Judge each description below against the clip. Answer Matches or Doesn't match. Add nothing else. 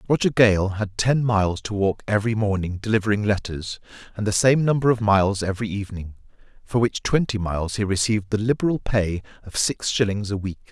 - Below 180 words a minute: Doesn't match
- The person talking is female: Doesn't match